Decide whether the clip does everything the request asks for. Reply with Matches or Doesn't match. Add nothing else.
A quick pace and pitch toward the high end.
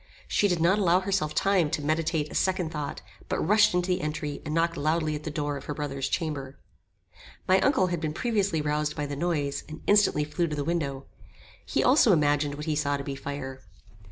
Doesn't match